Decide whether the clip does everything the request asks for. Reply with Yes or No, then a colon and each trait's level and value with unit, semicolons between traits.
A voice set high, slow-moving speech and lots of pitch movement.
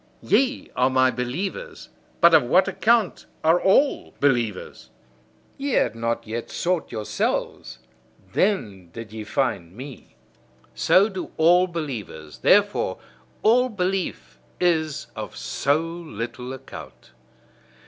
No: medium, 140 Hz; slow, 115 wpm; wide, 7.9 semitones